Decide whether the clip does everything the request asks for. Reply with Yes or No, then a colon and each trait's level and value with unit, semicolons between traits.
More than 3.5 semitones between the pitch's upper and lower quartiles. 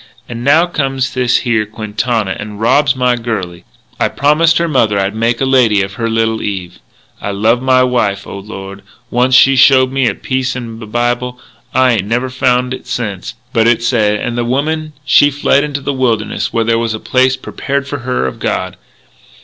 No: average, 3.0 semitones